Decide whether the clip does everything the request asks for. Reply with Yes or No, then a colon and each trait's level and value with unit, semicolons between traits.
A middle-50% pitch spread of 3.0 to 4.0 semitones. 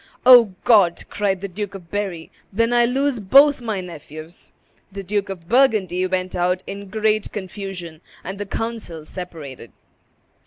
Yes: average, 3.4 semitones